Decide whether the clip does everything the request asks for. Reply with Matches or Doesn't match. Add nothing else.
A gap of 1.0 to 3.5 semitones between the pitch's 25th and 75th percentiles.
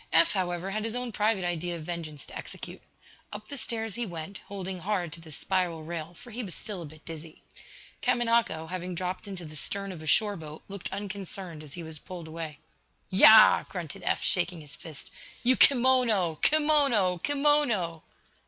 Doesn't match